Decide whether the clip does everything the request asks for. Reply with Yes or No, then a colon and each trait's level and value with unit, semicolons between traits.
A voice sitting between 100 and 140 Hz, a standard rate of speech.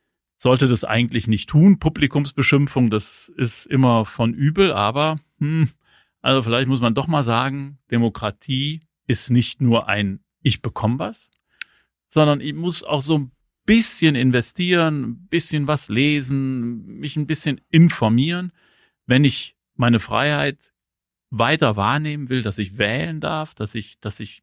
Yes: low, 135 Hz; average, 145 wpm